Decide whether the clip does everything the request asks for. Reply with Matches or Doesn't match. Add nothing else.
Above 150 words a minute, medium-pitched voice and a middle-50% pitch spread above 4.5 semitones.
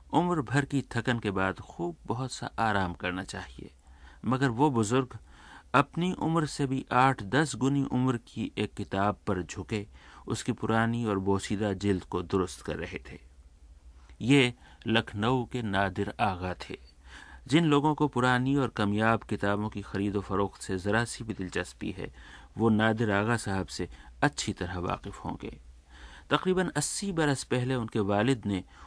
Doesn't match